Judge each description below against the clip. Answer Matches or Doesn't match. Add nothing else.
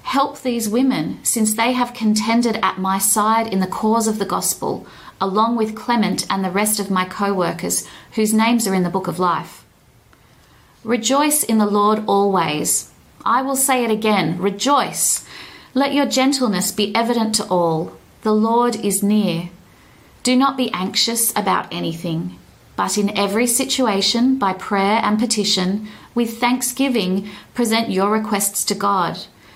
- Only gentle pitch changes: Doesn't match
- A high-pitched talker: Matches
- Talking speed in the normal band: Matches